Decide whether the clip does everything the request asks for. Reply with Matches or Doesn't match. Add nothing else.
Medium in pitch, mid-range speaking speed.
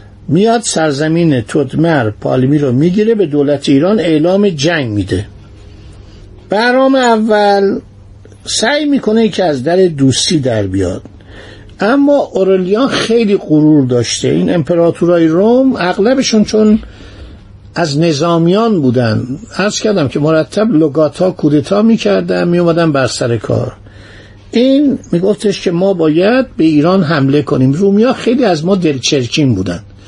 Matches